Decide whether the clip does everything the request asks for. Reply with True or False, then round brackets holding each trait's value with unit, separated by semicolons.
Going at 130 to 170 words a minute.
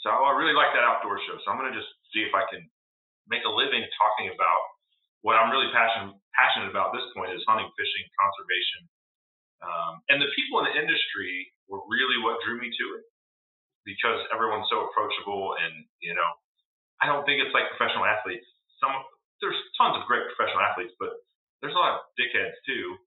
False (200 wpm)